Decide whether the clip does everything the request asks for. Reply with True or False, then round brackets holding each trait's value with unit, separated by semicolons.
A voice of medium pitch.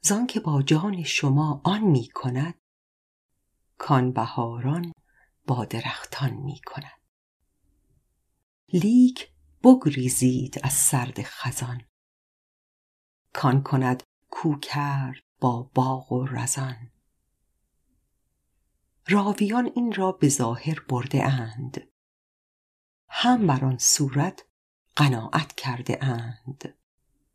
False (130 Hz)